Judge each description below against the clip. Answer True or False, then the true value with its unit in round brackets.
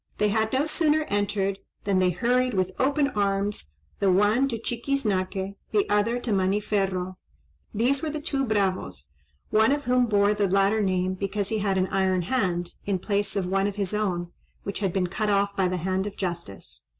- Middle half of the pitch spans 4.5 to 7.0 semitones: False (2.8 semitones)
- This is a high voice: True (200 Hz)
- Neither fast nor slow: True (190 wpm)